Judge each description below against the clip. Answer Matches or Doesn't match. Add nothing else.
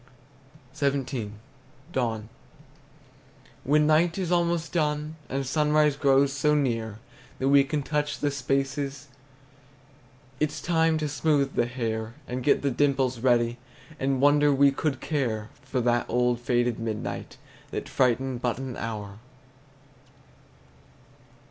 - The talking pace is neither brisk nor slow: Doesn't match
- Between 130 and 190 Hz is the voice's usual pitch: Matches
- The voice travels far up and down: Doesn't match